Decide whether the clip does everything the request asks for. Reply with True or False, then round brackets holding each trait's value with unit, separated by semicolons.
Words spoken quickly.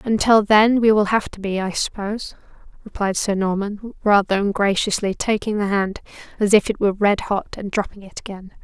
False (190 wpm)